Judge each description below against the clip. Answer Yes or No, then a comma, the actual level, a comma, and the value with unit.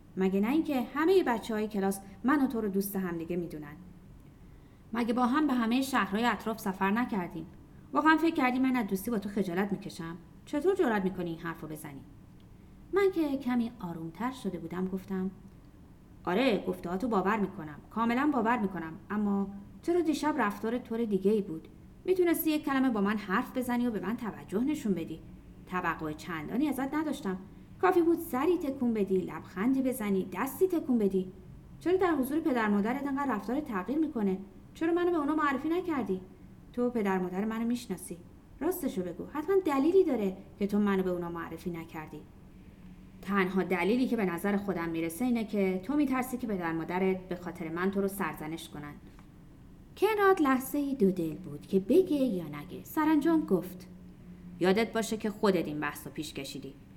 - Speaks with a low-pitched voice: No, high, 210 Hz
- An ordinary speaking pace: No, fast, 175 wpm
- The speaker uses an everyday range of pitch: No, wide, 6.5 semitones